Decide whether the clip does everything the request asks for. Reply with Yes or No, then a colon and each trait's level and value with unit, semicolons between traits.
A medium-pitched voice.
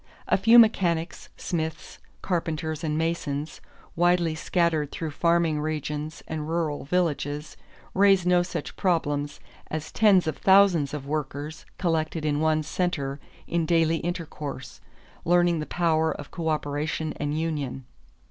Yes: medium, 160 Hz